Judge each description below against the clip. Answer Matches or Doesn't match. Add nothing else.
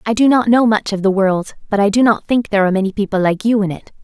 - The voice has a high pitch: Matches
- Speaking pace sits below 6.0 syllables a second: Doesn't match